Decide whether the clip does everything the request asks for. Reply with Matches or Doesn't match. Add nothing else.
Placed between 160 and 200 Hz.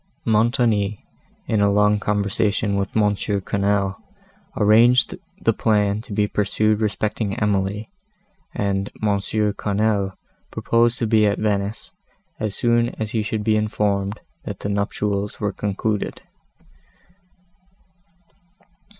Doesn't match